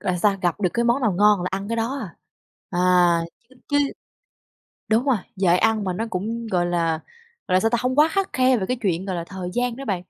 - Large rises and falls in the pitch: No, average, 4.8 semitones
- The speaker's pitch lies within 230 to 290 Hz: No, high, 210 Hz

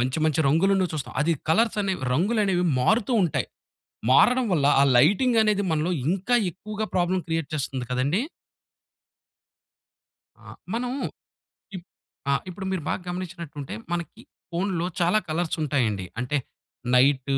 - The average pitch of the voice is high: No, medium, 175 Hz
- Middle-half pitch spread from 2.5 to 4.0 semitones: No, average, 5.2 semitones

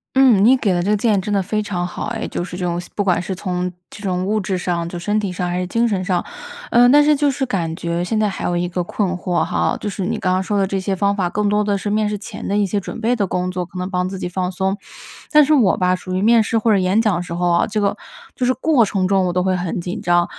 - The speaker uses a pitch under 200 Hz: Yes, high, 190 Hz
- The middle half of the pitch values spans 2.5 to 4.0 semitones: Yes, average, 2.8 semitones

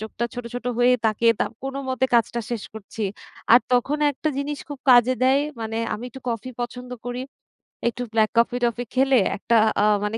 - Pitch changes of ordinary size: No, narrow, 2.0 semitones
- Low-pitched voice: No, high, 245 Hz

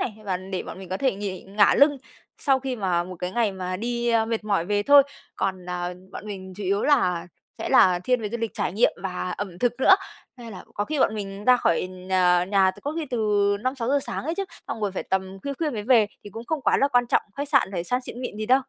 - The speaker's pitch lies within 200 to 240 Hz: Yes, high, 210 Hz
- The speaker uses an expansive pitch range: No, average, 4.9 semitones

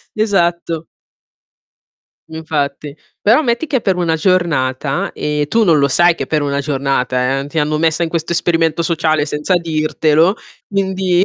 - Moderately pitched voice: Yes, medium, 160 Hz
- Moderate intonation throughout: Yes, average, 3.0 semitones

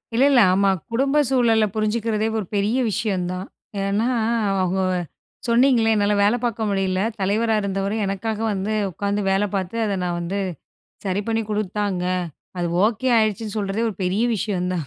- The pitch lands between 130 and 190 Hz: No, high, 205 Hz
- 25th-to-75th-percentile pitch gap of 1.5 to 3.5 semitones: Yes, narrow, 2.6 semitones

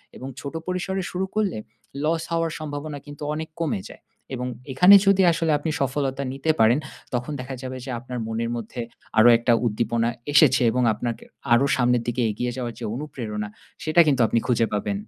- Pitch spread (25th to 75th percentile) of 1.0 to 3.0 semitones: No, average, 4.8 semitones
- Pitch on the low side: Yes, low, 130 Hz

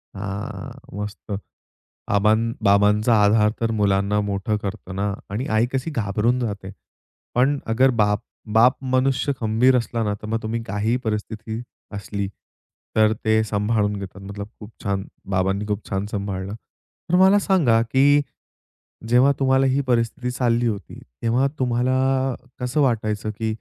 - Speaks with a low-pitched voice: Yes, low, 110 Hz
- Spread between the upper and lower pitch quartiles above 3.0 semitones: Yes, average, 3.4 semitones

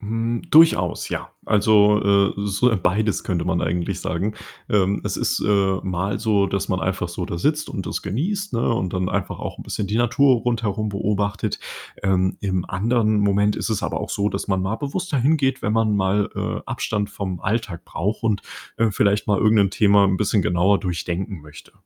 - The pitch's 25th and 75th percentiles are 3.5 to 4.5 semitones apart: No, average, 2.7 semitones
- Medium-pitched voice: No, low, 100 Hz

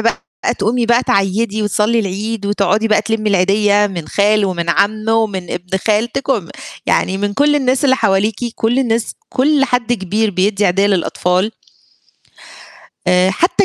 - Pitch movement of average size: Yes, average, 3.0 semitones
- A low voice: No, high, 210 Hz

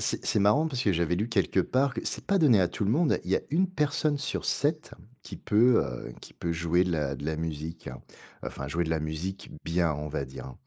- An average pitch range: No, wide, 8.5 semitones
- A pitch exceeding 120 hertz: No, very low, 90 Hz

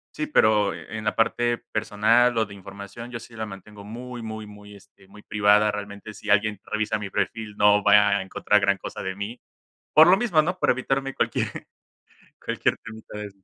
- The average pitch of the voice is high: No, low, 105 Hz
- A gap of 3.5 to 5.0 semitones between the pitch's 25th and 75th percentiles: No, narrow, 2.4 semitones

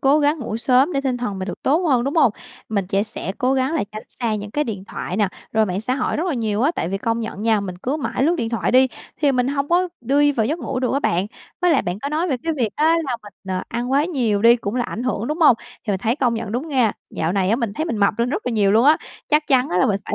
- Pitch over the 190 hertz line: Yes, high, 245 Hz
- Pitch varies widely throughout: No, average, 4.9 semitones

